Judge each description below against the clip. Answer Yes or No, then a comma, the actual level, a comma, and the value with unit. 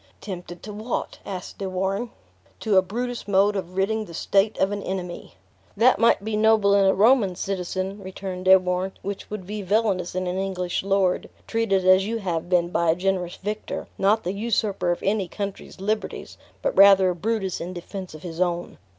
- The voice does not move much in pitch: Yes, narrow, 2.3 semitones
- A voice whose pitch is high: Yes, high, 195 Hz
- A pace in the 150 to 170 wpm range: No, average, 195 wpm